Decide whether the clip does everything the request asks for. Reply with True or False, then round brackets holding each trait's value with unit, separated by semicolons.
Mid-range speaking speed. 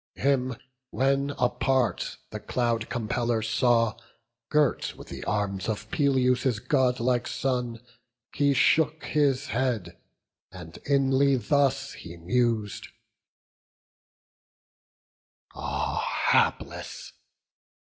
False (85 wpm)